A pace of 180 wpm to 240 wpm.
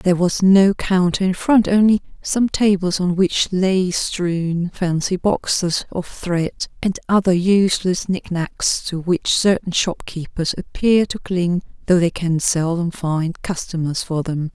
No: average, 155 wpm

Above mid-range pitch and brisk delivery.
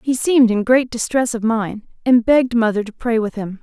Yes: high, 235 Hz; fast, 230 wpm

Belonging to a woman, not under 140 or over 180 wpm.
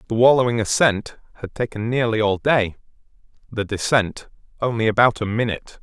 No: male; average, 145 wpm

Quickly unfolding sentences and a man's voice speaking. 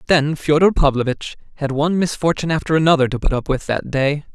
No: average, 195 wpm; male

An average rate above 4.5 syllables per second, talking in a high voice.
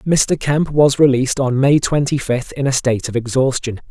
No: 5.0 syllables/s; low, 135 Hz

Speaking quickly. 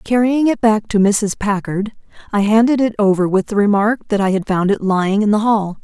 Yes: fast, 225 wpm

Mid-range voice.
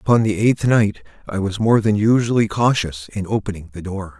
No: low, 105 Hz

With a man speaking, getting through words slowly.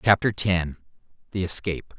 Yes: male; slow, 120 wpm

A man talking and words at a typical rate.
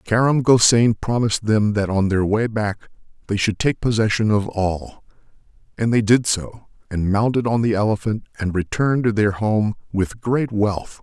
Yes: male; average, 175 wpm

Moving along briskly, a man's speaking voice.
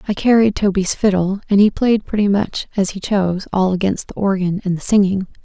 No: fast, 210 wpm; female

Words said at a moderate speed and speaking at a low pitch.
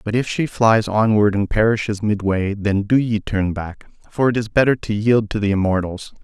No: fast, 210 wpm; low, 105 Hz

